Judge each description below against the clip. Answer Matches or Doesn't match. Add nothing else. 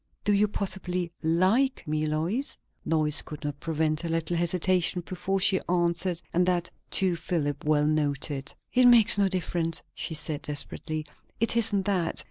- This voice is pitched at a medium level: Matches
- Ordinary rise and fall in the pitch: Matches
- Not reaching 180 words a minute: Matches